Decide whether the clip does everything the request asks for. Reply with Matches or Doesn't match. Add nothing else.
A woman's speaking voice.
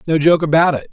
Doesn't match